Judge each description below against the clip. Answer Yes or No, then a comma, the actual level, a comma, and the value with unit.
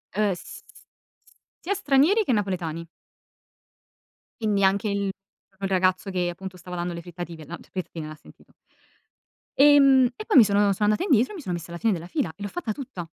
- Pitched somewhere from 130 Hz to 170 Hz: No, high, 200 Hz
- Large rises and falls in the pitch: Yes, wide, 6.5 semitones